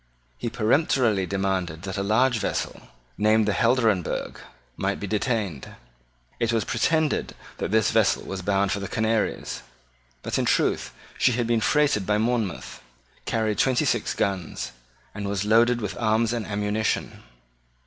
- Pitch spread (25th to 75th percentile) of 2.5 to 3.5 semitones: Yes, average, 2.8 semitones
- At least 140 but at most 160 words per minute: Yes, average, 150 wpm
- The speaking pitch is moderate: No, low, 110 Hz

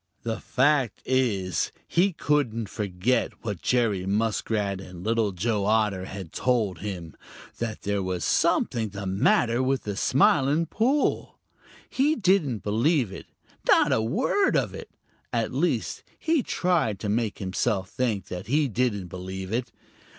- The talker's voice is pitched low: Yes, low, 110 Hz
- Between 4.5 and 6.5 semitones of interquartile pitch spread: Yes, average, 5.1 semitones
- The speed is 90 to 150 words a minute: Yes, average, 145 wpm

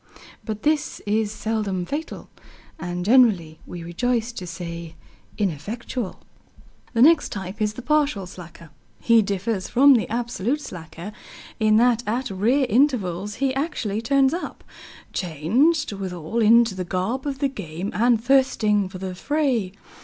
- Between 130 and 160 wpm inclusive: Yes, average, 140 wpm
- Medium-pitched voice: No, high, 215 Hz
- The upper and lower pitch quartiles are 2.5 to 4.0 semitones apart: No, wide, 5.6 semitones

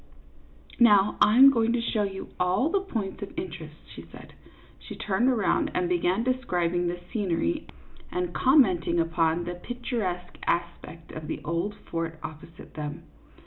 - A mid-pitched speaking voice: Yes, medium, 180 Hz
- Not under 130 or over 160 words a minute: Yes, average, 155 wpm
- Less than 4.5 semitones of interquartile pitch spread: No, average, 5.1 semitones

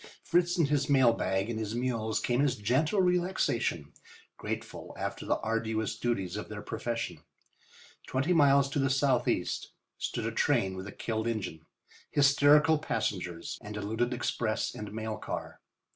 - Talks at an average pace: Yes, average, 155 wpm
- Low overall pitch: Yes, low, 120 Hz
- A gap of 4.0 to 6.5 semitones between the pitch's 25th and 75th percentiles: Yes, average, 4.5 semitones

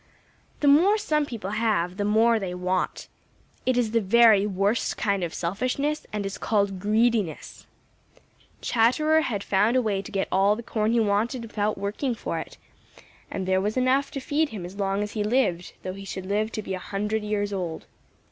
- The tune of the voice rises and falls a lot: No, average, 3.3 semitones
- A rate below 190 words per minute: No, average, 195 wpm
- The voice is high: Yes, high, 210 Hz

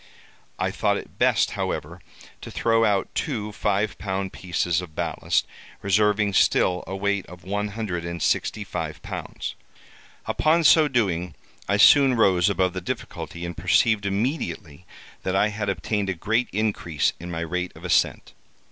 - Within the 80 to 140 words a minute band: No, average, 155 wpm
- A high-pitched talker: No, low, 100 Hz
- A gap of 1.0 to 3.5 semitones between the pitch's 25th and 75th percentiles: Yes, average, 3.1 semitones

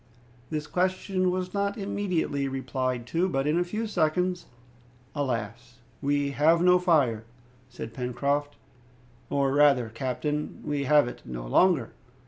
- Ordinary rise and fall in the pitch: No, wide, 5.7 semitones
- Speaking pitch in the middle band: Yes, medium, 145 Hz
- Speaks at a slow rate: Yes, slow, 130 wpm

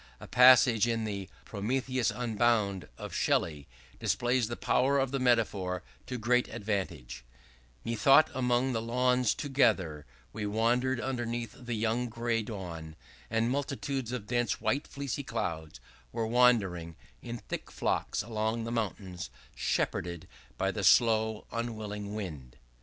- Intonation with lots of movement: No, average, 3.5 semitones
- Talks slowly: Yes, slow, 130 wpm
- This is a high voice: No, low, 115 Hz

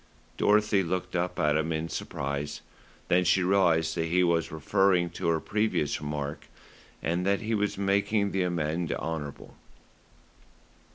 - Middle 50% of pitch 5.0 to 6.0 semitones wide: No, average, 3.5 semitones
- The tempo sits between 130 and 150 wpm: Yes, average, 145 wpm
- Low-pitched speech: Yes, very low, 90 Hz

